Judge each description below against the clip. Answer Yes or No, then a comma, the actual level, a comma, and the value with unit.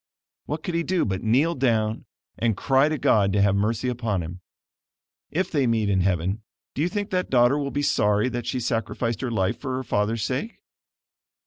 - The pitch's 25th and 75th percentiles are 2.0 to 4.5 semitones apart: No, average, 5.2 semitones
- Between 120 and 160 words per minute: No, average, 200 wpm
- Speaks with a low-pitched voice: Yes, low, 120 Hz